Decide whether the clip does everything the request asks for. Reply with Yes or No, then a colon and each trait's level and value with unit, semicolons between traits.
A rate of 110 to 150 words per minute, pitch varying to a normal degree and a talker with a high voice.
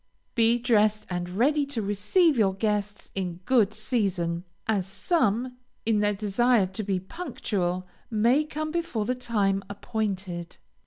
Yes: average, 140 wpm; average, 4.0 semitones; high, 210 Hz